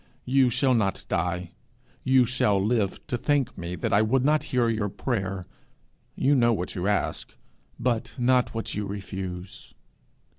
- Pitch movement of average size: Yes, average, 4.7 semitones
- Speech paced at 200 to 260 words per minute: No, average, 155 wpm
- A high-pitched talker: No, low, 110 Hz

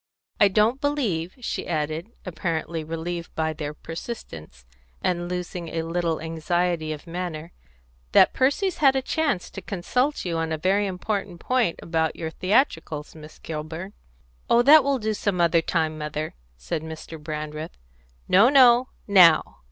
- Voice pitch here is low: No, medium, 175 Hz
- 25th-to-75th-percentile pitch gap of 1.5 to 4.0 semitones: No, average, 4.6 semitones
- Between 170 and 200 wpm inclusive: No, average, 150 wpm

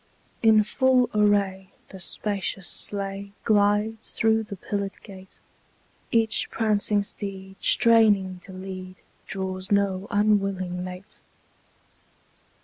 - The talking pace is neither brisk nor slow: No, slow, 100 wpm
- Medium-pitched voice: No, high, 200 Hz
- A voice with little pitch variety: Yes, narrow, 2.0 semitones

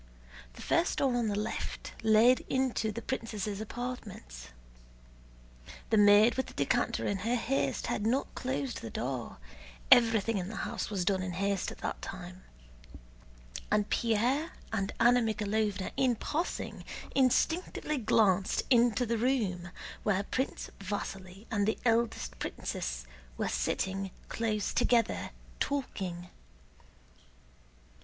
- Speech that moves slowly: Yes, slow, 125 wpm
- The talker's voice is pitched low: No, high, 215 Hz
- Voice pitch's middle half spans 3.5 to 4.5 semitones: Yes, average, 3.9 semitones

